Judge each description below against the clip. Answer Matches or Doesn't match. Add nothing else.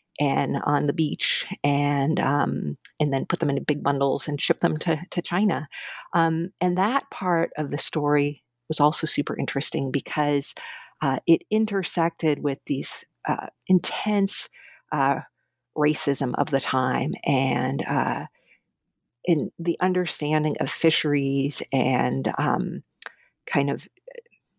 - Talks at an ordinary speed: Doesn't match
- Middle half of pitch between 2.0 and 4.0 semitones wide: Matches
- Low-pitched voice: Doesn't match